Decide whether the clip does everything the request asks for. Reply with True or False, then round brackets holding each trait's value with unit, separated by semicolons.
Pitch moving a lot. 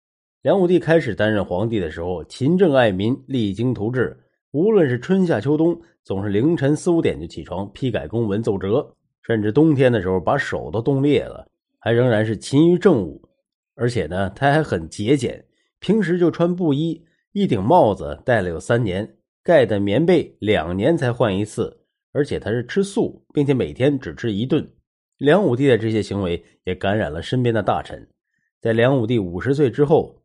True (6.8 semitones)